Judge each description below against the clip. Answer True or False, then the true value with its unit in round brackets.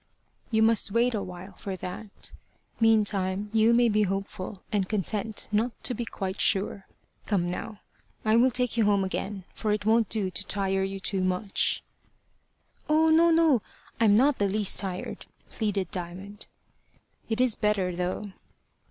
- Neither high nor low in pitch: False (210 Hz)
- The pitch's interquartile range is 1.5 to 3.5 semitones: True (2.7 semitones)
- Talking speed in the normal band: True (160 wpm)